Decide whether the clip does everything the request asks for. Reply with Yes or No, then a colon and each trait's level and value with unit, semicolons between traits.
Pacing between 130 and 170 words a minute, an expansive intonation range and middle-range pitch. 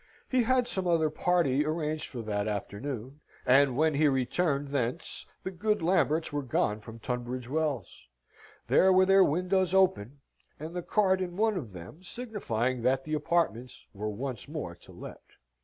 Yes: average, 165 wpm; wide, 6.6 semitones; medium, 150 Hz